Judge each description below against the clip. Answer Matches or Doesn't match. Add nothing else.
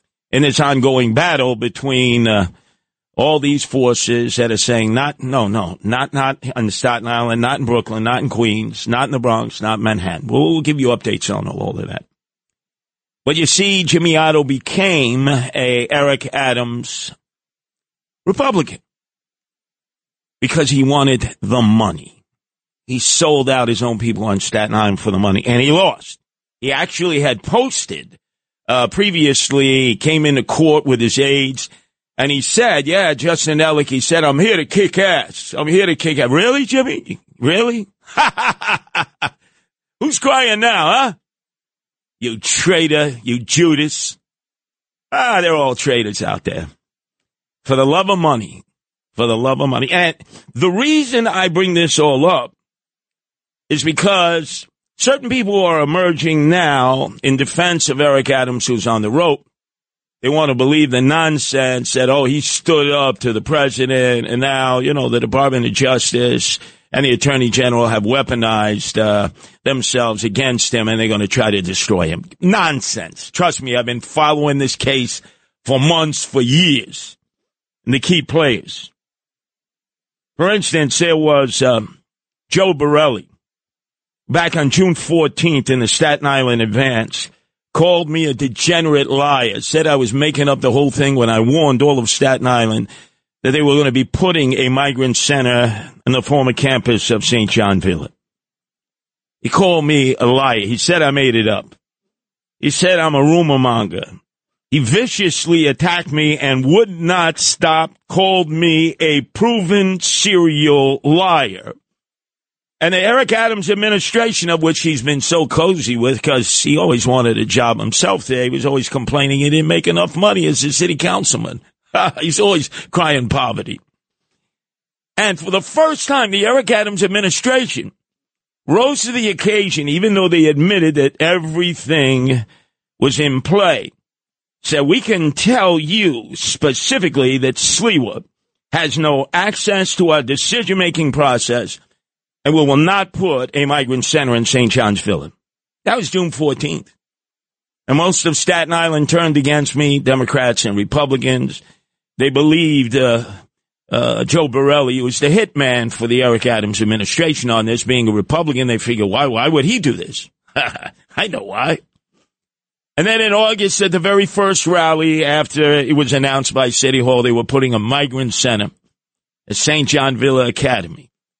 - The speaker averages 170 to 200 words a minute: Doesn't match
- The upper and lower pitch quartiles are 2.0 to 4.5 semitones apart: Doesn't match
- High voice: Doesn't match